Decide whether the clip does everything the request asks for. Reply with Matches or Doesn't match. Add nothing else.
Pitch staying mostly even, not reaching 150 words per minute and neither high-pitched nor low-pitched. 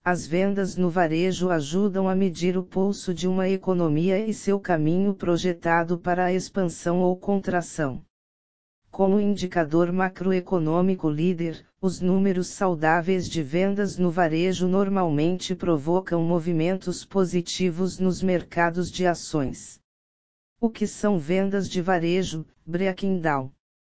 Matches